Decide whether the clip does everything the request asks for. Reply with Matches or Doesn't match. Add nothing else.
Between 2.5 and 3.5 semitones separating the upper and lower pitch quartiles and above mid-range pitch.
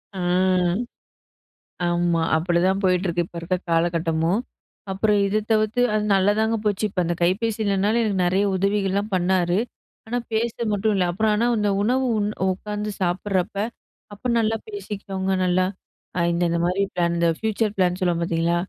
Matches